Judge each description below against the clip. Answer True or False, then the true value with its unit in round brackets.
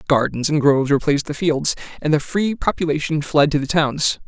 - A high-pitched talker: False (150 Hz)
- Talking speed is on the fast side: False (195 wpm)